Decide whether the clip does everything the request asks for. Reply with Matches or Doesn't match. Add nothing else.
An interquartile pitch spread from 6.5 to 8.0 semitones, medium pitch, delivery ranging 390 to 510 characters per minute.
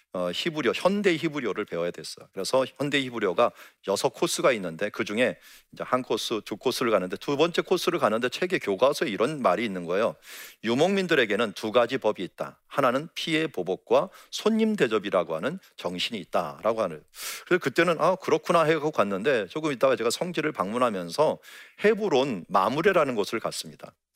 Matches